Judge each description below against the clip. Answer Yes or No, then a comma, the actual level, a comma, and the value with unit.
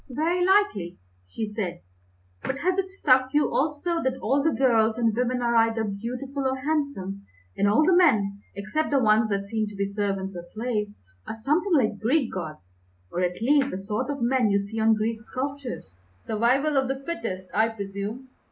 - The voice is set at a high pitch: Yes, high, 230 Hz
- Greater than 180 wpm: Yes, average, 190 wpm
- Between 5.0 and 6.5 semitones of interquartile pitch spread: Yes, wide, 5.4 semitones